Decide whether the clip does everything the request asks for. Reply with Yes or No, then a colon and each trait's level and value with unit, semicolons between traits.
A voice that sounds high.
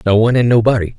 No: low, 115 Hz